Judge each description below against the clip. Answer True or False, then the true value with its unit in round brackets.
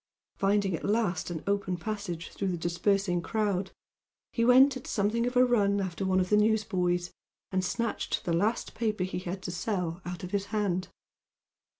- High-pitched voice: True (195 Hz)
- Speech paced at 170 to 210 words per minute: True (180 wpm)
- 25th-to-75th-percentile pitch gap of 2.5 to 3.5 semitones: True (3.1 semitones)